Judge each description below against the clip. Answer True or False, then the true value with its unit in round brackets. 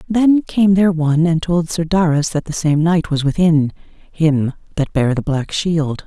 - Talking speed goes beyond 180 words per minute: True (200 wpm)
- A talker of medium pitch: True (165 Hz)